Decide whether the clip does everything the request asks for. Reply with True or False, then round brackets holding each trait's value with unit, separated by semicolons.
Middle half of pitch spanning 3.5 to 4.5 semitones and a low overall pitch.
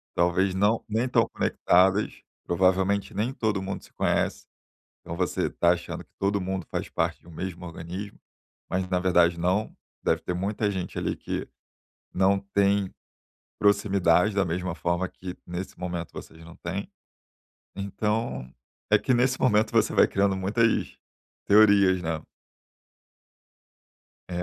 False (2.5 semitones; 95 Hz)